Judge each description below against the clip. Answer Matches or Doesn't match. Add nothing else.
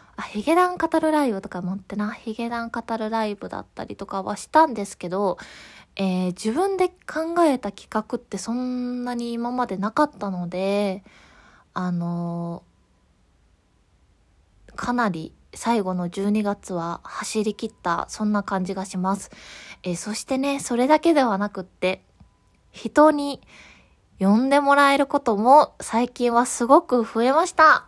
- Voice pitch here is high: Matches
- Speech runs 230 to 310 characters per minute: Matches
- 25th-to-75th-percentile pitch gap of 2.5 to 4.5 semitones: Doesn't match